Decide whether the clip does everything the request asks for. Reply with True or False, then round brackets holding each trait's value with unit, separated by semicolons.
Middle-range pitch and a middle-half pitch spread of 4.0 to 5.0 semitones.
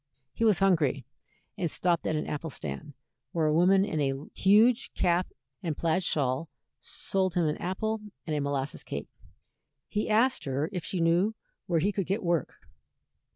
True (170 Hz; 4.5 semitones)